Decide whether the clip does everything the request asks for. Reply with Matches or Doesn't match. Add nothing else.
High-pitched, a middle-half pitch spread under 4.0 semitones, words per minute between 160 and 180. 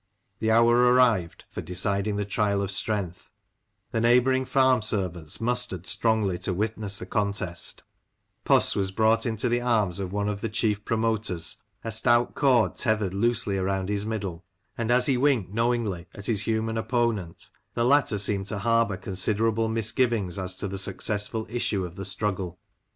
Doesn't match